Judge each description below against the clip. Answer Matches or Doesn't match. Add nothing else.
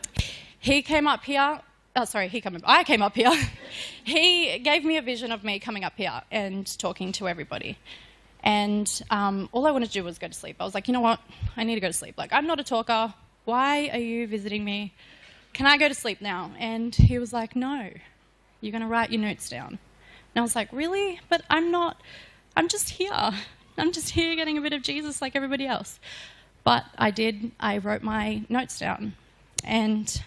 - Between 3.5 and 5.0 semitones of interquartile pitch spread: Doesn't match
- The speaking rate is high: Matches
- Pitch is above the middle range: Matches